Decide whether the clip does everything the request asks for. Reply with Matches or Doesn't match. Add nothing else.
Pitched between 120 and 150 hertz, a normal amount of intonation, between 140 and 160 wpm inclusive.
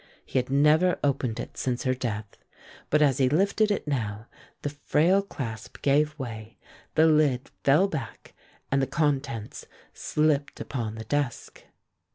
Matches